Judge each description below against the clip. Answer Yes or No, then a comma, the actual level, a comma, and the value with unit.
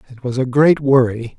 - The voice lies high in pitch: No, low, 130 Hz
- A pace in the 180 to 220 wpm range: Yes, fast, 215 wpm